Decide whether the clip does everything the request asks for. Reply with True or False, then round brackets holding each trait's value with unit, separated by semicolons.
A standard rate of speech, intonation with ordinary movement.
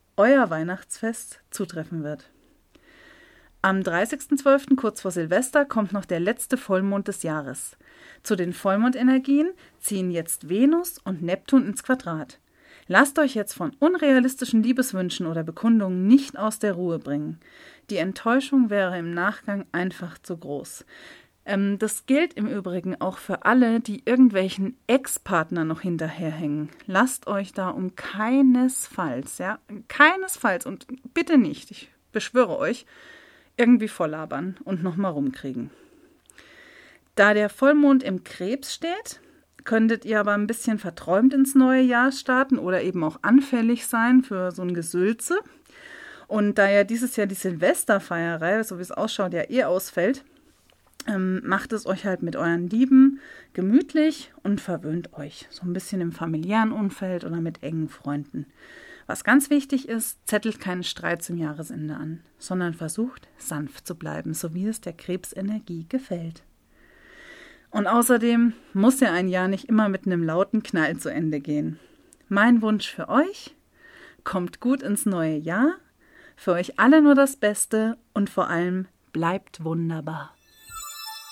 False (140 wpm; 6.6 semitones)